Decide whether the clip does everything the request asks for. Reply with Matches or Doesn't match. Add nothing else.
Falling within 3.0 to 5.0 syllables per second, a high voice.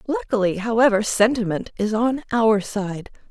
Matches